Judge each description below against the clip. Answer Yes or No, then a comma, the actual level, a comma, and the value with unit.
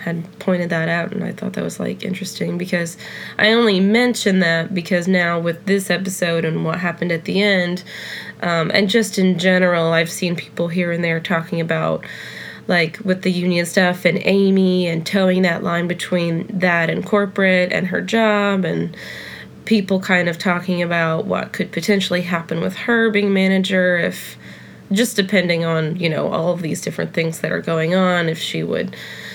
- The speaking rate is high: No, average, 185 wpm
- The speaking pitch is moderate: Yes, medium, 180 Hz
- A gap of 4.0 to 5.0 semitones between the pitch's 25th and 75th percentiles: No, narrow, 2.5 semitones